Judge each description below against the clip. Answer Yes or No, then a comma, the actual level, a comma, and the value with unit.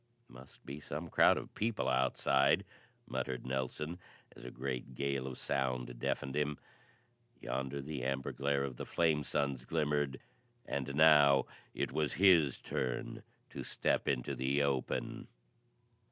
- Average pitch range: No, narrow, 2.2 semitones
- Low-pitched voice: Yes, very low, 70 Hz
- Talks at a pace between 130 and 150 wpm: Yes, average, 140 wpm